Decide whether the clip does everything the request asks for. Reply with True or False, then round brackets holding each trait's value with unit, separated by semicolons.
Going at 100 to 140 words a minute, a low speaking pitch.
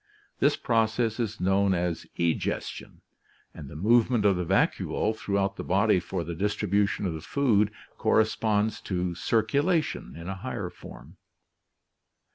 True (135 wpm; 100 Hz)